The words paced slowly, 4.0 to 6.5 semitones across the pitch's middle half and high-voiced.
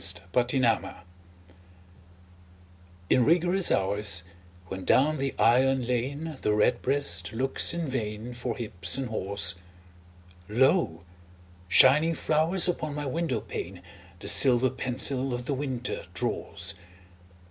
No: slow, 110 wpm; average, 5.1 semitones; low, 125 Hz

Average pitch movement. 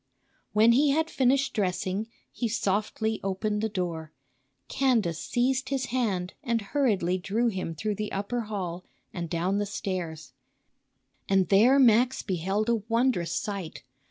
Yes: average, 4.6 semitones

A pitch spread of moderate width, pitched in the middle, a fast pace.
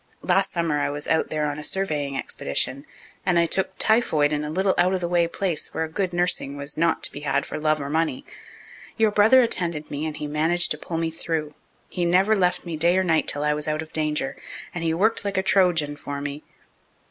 Yes: average, 3.3 semitones; medium, 160 Hz; fast, 230 wpm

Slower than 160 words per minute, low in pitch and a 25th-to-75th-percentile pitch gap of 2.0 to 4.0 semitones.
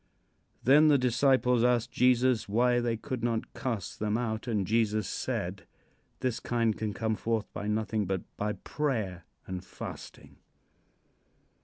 Yes: average, 145 wpm; low, 115 Hz; narrow, 2.6 semitones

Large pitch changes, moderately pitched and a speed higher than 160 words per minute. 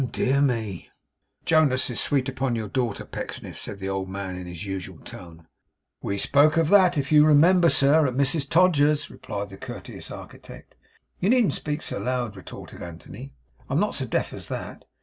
No: wide, 7.2 semitones; low, 130 Hz; average, 185 wpm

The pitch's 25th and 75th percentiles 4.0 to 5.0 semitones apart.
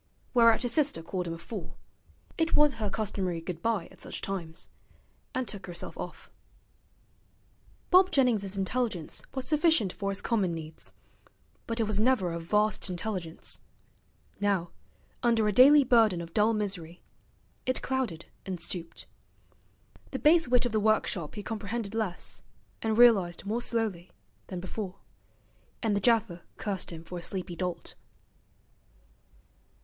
Yes: average, 4.6 semitones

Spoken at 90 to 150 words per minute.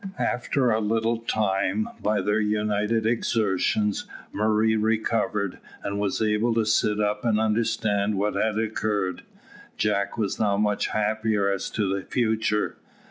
Yes: slow, 135 wpm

